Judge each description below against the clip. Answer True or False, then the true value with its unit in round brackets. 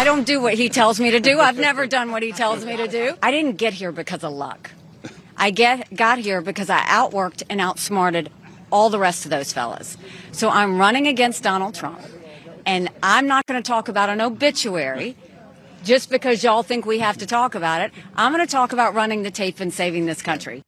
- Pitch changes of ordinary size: True (4.8 semitones)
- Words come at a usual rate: False (225 wpm)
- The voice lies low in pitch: False (210 Hz)